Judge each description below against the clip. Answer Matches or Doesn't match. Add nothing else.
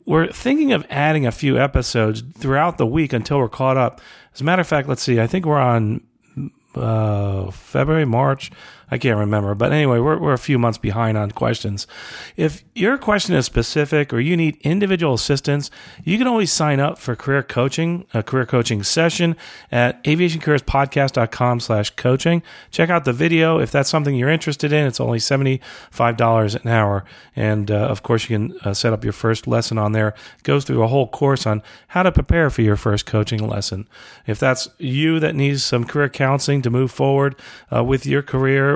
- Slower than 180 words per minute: Doesn't match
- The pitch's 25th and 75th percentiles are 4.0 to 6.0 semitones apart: Matches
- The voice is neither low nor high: Doesn't match